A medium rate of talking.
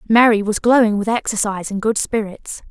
Yes: average, 175 wpm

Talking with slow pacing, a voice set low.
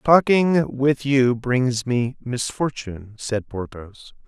Yes: slow, 110 wpm; low, 125 Hz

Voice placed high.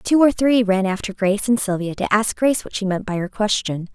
Yes: high, 210 Hz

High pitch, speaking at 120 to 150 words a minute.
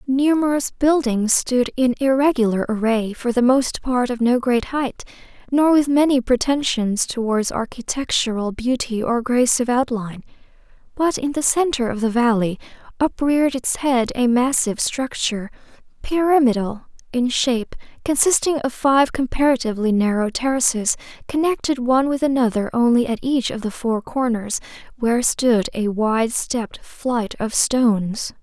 Yes: high, 245 Hz; average, 140 wpm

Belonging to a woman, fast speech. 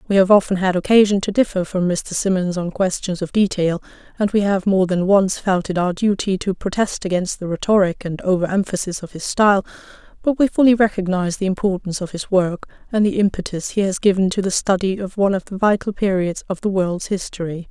Yes: female; fast, 215 wpm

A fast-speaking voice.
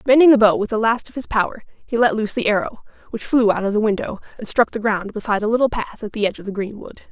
Yes: fast, 285 wpm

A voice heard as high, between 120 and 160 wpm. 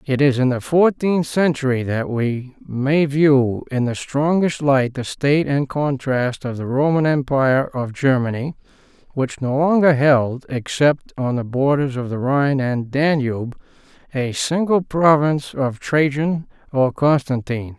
No: low, 135 Hz; average, 150 wpm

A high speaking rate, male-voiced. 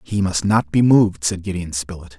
Yes: fast, 220 wpm; male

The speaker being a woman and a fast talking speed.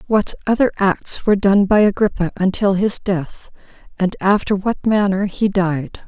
No: female; average, 160 wpm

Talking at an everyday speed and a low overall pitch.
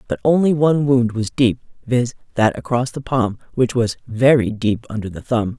Yes: average, 195 wpm; low, 120 Hz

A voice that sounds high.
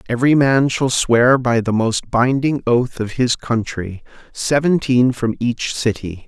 No: low, 120 Hz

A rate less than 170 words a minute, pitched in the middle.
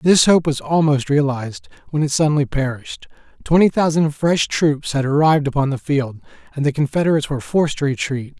No: average, 180 wpm; medium, 145 Hz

